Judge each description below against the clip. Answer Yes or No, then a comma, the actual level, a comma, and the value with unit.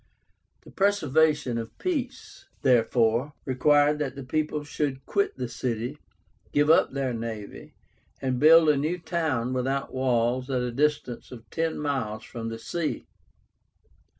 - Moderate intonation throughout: Yes, average, 3.7 semitones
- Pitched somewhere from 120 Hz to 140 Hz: Yes, low, 135 Hz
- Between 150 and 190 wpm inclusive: No, average, 140 wpm